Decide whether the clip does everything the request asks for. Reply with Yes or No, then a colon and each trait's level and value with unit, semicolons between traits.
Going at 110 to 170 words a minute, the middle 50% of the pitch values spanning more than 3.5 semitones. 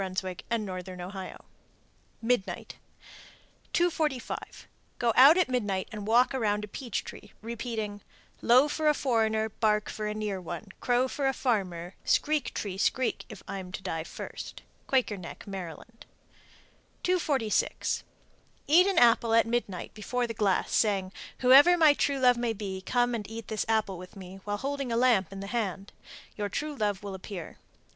Yes: average, 160 wpm; average, 4.3 semitones